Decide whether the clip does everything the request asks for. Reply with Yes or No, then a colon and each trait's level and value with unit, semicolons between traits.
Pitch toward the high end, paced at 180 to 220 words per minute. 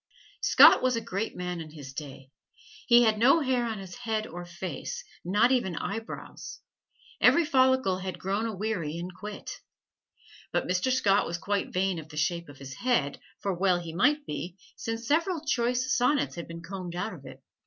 Yes: high, 195 Hz; average, 185 wpm